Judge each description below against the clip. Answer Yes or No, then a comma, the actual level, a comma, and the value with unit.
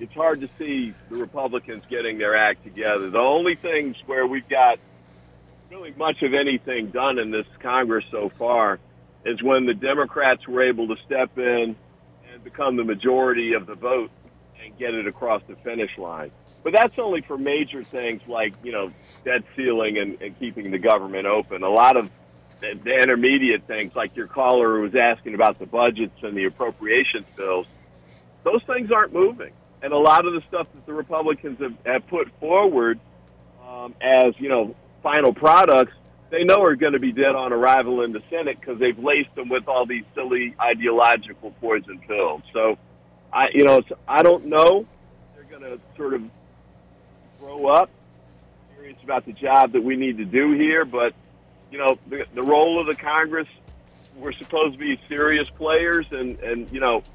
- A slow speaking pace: No, average, 185 wpm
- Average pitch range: No, wide, 6.1 semitones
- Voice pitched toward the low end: Yes, low, 125 Hz